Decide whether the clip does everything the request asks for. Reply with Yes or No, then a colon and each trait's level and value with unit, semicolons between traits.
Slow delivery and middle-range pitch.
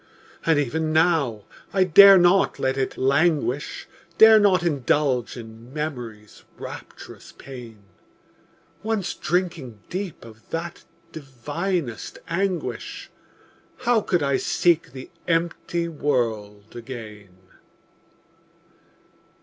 Yes: slow, 95 wpm; medium, 150 Hz